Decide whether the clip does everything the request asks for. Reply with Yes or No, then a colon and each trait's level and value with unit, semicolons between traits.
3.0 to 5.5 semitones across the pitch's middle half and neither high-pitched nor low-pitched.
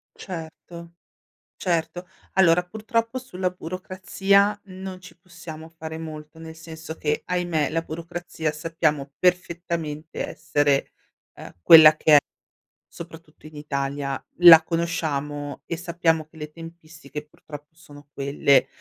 No: narrow, 2.5 semitones; medium, 165 Hz